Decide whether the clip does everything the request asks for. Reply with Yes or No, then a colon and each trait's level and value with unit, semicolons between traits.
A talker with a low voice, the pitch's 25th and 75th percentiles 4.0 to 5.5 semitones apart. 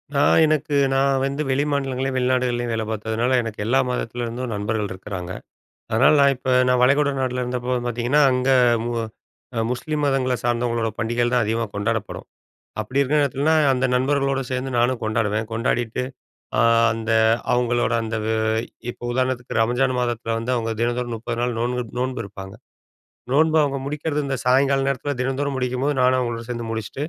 No: low, 125 Hz; narrow, 2.6 semitones